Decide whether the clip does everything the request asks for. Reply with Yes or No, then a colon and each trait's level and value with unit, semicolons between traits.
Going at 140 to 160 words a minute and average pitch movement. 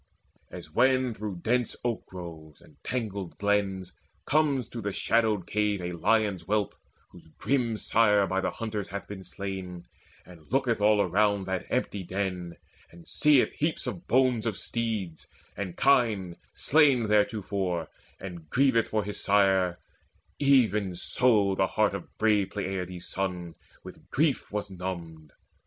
Yes: average, 145 wpm; average, 3.9 semitones